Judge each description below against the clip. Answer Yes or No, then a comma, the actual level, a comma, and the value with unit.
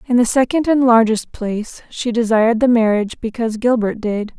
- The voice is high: Yes, high, 230 Hz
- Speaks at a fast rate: No, average, 180 wpm